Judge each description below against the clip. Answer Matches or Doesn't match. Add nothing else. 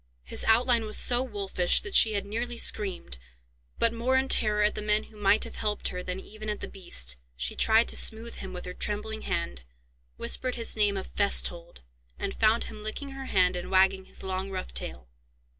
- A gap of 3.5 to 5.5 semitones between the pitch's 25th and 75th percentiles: Doesn't match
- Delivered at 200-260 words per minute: Matches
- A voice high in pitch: Matches